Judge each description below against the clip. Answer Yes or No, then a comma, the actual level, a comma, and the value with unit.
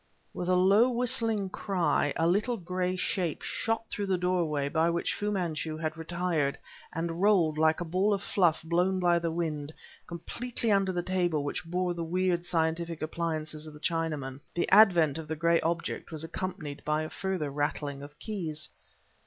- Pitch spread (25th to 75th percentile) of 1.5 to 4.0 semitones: Yes, average, 2.9 semitones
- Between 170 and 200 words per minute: Yes, average, 175 wpm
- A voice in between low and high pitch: Yes, medium, 170 Hz